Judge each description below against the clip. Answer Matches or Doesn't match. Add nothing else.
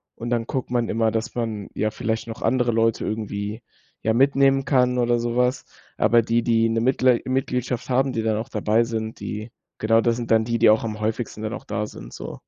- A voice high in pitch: Doesn't match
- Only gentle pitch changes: Matches